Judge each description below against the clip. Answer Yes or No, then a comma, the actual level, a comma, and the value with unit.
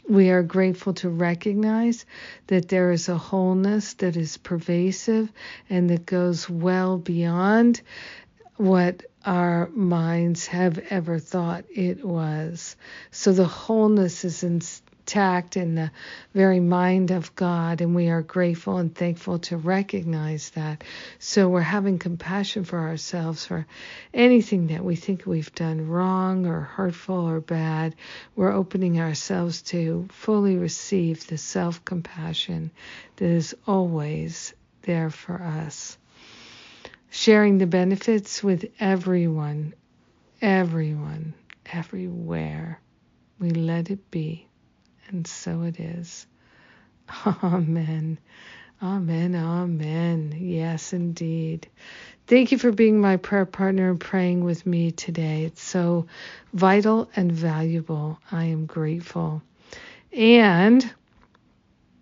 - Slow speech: Yes, slow, 115 wpm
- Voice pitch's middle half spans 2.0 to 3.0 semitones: Yes, narrow, 2.5 semitones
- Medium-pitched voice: Yes, medium, 175 Hz